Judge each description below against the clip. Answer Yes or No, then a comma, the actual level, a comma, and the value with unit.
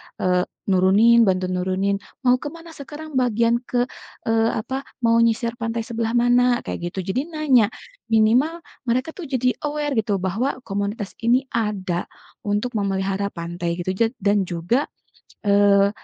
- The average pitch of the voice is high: Yes, high, 225 Hz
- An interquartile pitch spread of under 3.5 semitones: No, average, 4.1 semitones